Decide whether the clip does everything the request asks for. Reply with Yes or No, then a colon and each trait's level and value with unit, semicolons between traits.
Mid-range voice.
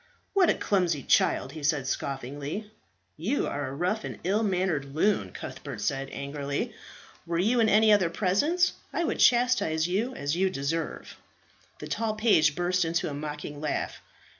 Yes: medium, 170 Hz